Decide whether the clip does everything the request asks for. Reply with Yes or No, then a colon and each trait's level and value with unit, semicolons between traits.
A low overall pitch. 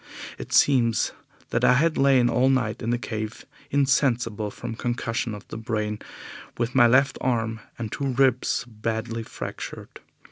Yes: low, 120 Hz